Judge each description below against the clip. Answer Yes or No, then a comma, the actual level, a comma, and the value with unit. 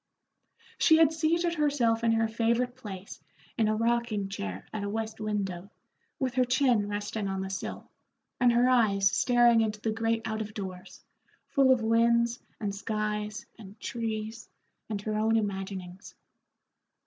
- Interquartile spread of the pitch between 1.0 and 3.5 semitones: Yes, narrow, 2.5 semitones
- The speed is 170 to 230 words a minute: No, average, 155 wpm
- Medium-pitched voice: No, high, 220 Hz